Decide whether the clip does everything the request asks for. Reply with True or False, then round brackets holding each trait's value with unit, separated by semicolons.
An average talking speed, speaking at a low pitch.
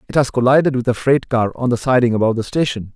False (265 wpm; 125 Hz)